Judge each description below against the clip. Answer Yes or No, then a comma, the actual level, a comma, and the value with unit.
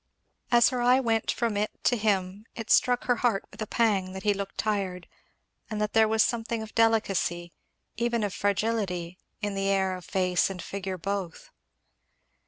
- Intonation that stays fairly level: No, average, 3.0 semitones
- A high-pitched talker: Yes, high, 205 Hz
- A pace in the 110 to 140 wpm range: No, average, 185 wpm